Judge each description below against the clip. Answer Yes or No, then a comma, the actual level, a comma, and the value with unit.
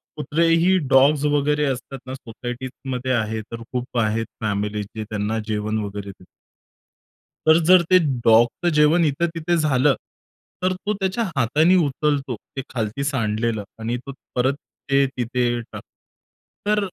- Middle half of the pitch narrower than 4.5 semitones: No, average, 5.1 semitones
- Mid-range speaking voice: No, low, 130 Hz